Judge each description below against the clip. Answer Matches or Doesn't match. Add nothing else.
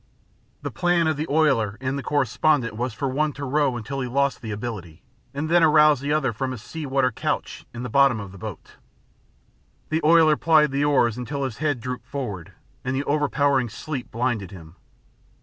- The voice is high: Doesn't match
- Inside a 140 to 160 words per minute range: Doesn't match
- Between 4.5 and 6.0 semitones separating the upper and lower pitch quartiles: Doesn't match